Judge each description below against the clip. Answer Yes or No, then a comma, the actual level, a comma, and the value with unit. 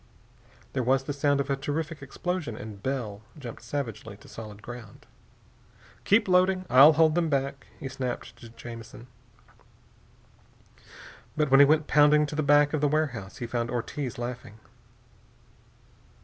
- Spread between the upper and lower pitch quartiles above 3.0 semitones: Yes, average, 4.0 semitones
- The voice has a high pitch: No, low, 135 Hz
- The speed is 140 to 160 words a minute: Yes, average, 150 wpm